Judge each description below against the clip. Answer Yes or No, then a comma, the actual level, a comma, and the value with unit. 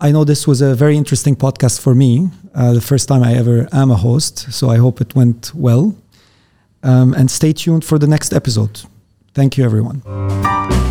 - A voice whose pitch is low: Yes, low, 130 Hz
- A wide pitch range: No, average, 4.1 semitones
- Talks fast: Yes, fast, 200 wpm